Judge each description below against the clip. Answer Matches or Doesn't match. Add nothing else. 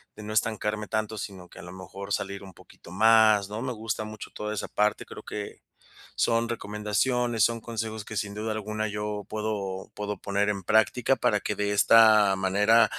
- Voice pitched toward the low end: Matches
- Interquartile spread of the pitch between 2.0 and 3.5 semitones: Doesn't match